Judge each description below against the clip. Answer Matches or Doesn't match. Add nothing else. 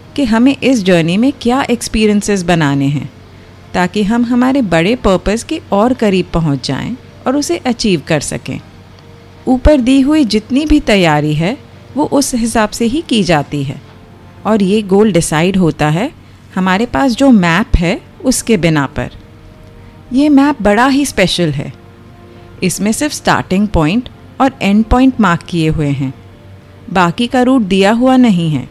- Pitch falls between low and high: Doesn't match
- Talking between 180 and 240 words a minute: Doesn't match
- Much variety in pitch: Matches